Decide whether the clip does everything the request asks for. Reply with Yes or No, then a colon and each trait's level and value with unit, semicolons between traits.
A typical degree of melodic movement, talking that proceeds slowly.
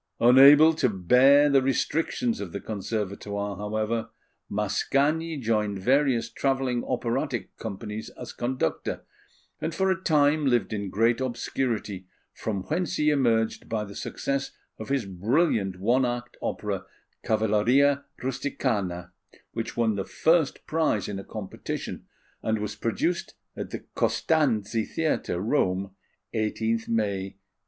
Yes: average, 4.9 semitones; slow, 130 wpm